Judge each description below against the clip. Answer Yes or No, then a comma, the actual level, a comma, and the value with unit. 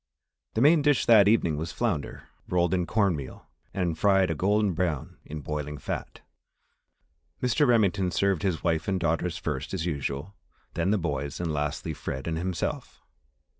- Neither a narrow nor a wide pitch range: Yes, average, 4.5 semitones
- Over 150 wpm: Yes, average, 165 wpm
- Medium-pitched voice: No, very low, 85 Hz